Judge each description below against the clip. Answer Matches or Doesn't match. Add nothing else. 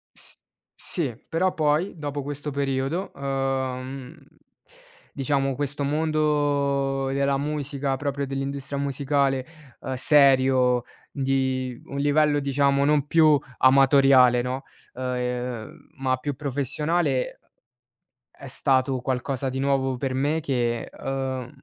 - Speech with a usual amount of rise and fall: Doesn't match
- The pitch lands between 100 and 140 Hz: Matches